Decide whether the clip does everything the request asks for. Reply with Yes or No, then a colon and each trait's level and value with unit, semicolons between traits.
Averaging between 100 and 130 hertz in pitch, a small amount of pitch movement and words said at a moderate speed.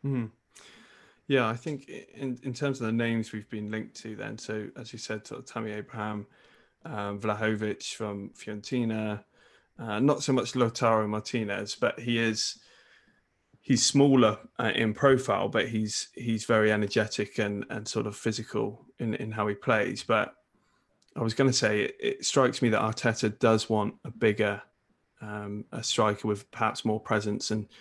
Yes: low, 110 Hz; narrow, 2.3 semitones; average, 170 wpm